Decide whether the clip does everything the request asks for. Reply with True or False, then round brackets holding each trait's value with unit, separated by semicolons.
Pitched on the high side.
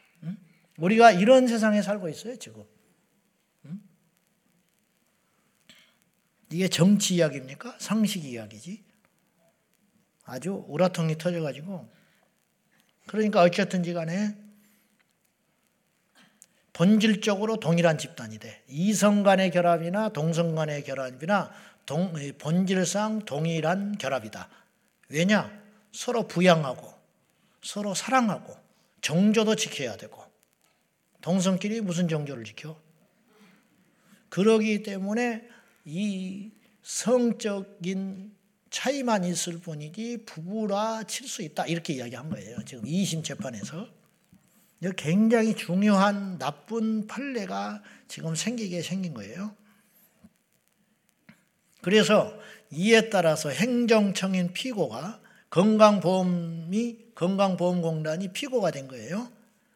True (195 Hz)